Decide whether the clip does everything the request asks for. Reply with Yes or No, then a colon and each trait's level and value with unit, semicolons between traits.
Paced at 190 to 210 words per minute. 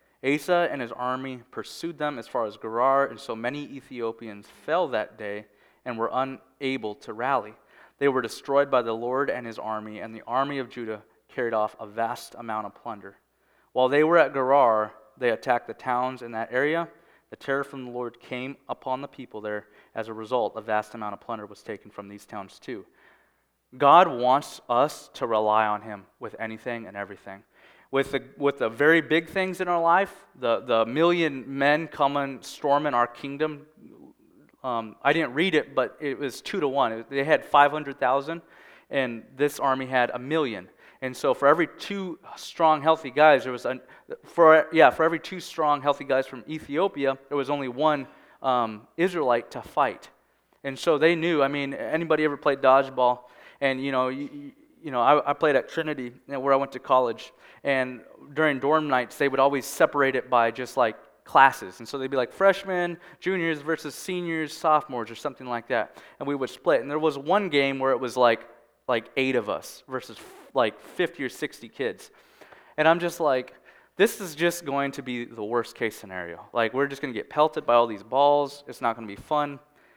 Yes: fast, 205 wpm